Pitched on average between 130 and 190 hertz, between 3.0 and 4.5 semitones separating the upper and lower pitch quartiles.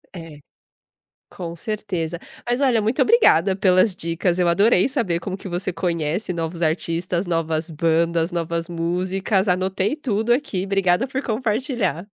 Yes: medium, 185 Hz; average, 4.1 semitones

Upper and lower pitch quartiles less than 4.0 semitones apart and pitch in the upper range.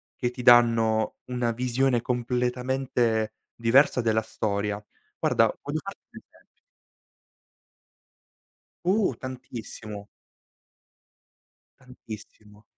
No: narrow, 2.4 semitones; low, 120 Hz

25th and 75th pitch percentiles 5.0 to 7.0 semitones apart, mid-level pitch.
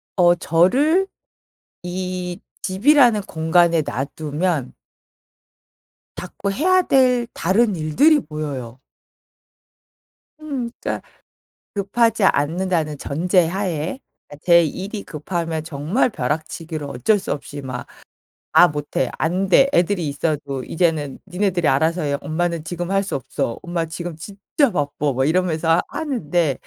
No: average, 4.4 semitones; medium, 175 Hz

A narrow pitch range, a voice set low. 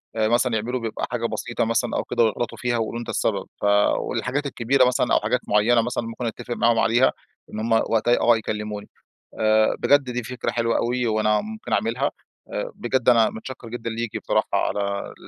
Yes: narrow, 1.9 semitones; low, 115 Hz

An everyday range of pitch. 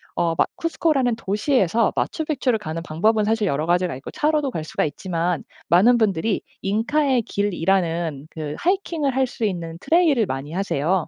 No: wide, 7.6 semitones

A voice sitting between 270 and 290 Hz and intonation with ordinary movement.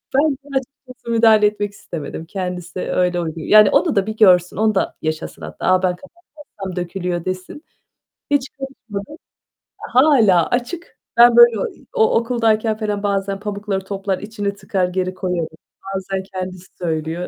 No: high, 200 Hz; average, 3.9 semitones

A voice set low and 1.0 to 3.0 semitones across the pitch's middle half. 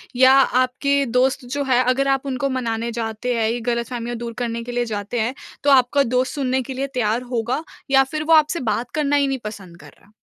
No: very high, 250 Hz; narrow, 2.6 semitones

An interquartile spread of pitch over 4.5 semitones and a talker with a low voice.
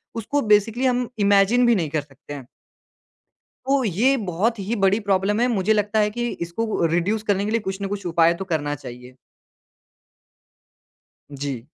No: average, 5.2 semitones; high, 200 Hz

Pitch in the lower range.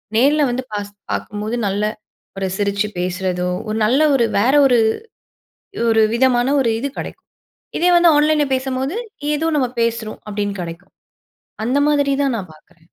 No: high, 230 Hz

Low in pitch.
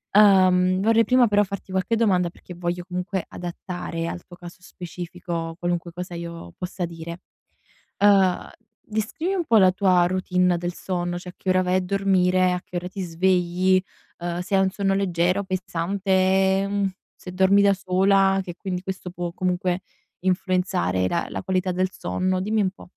No: medium, 185 Hz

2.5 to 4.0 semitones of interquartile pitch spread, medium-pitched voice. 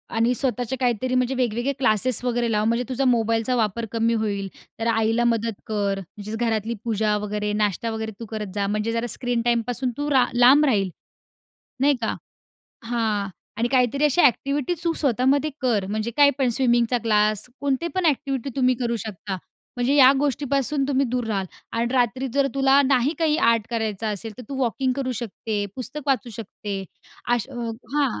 No: average, 3.1 semitones; high, 240 Hz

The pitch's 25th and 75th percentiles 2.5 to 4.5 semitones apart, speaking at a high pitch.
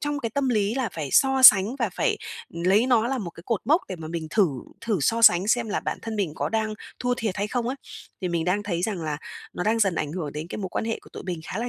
No: average, 4.9 semitones; high, 210 Hz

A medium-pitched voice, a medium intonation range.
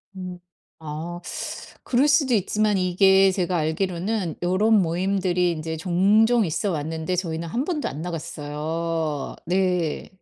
Yes: medium, 180 Hz; average, 3.3 semitones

